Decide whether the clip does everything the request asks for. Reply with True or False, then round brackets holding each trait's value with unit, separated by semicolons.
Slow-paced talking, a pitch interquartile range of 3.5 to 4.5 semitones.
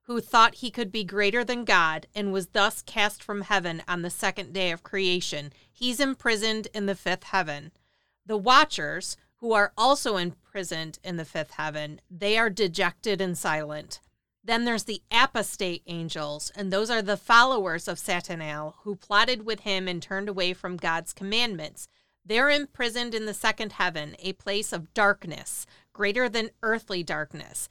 False (165 wpm; 4.1 semitones)